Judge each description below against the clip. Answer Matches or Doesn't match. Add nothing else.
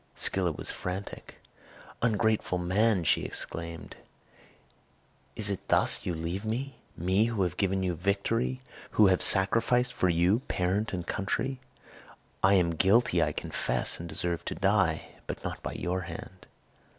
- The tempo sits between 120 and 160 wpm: Matches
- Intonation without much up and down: Doesn't match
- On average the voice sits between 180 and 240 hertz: Doesn't match